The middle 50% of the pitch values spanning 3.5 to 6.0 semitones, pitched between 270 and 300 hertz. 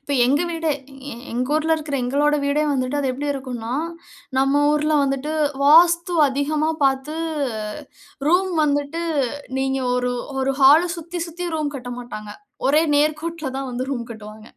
No: average, 2.9 semitones; very high, 285 Hz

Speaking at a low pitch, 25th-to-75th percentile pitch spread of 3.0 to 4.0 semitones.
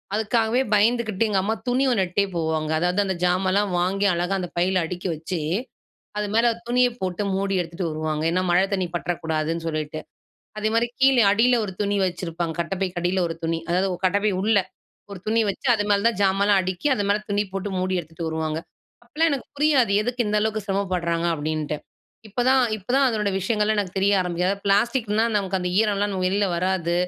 No: high, 195 Hz; average, 3.4 semitones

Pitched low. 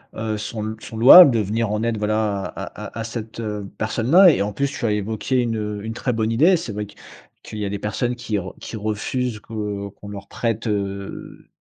Yes: low, 110 Hz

